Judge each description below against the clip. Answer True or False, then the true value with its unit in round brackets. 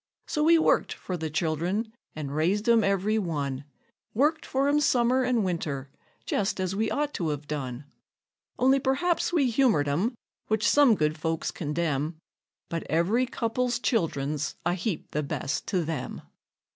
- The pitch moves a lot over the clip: True (8.0 semitones)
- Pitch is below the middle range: False (185 Hz)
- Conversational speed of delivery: True (160 wpm)